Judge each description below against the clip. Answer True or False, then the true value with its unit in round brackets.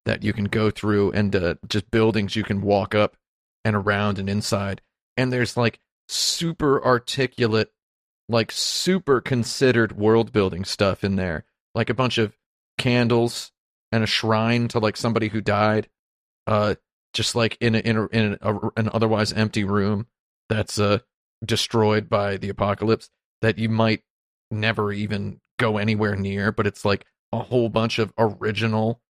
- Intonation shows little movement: True (1.9 semitones)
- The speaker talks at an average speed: True (165 wpm)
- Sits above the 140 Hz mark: False (110 Hz)